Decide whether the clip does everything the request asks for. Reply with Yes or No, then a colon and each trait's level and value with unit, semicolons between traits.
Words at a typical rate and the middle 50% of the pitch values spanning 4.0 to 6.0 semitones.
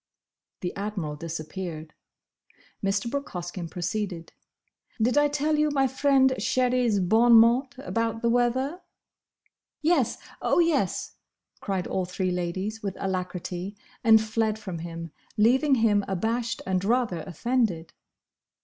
No: slow, 125 wpm; wide, 5.5 semitones